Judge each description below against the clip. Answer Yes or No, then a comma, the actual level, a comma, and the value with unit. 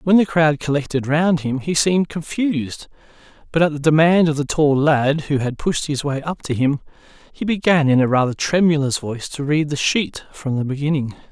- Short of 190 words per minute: No, fast, 205 wpm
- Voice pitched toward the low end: No, medium, 150 Hz